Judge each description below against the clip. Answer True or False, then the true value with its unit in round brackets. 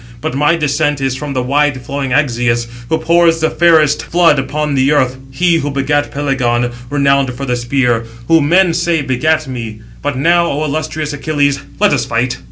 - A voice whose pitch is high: False (145 Hz)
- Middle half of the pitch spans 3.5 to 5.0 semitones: False (3.1 semitones)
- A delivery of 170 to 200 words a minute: True (180 wpm)